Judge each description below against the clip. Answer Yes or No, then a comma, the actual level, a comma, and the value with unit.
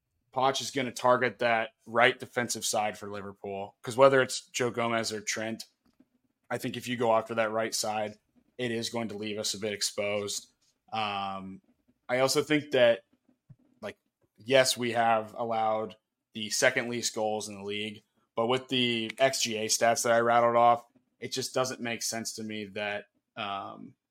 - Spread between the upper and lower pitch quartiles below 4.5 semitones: Yes, average, 2.9 semitones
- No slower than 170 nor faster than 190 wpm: Yes, average, 175 wpm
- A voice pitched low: Yes, low, 115 Hz